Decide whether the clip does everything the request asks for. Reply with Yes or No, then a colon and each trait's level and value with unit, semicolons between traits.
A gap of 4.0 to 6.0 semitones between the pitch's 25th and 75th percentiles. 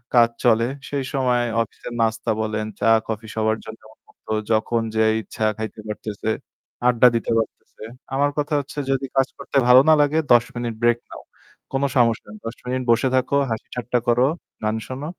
No: average, 2.8 semitones